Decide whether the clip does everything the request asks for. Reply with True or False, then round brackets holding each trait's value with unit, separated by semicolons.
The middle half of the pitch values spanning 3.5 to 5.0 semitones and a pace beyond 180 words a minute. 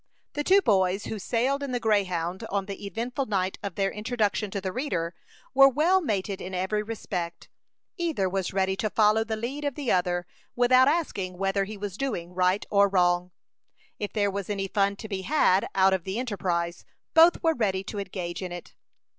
True (4.1 semitones; 195 wpm)